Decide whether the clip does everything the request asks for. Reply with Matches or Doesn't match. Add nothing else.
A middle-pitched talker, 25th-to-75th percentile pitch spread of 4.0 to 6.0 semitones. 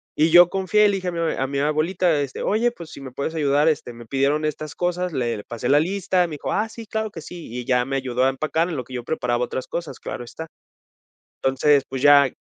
Matches